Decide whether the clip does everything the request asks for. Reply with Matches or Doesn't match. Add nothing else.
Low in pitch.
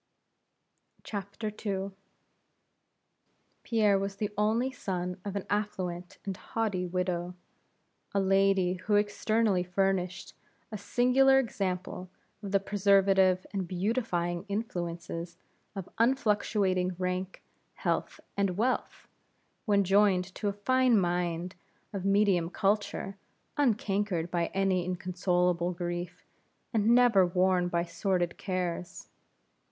Doesn't match